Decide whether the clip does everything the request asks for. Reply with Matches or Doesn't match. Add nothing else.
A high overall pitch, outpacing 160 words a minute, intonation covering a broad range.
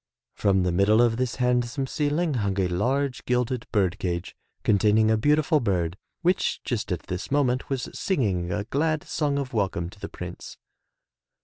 Doesn't match